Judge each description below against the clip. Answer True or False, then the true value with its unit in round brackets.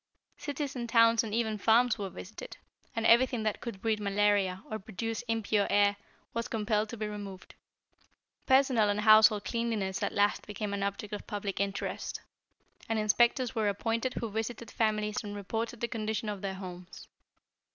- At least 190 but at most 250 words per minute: False (165 wpm)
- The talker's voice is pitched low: False (215 Hz)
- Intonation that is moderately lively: False (2.0 semitones)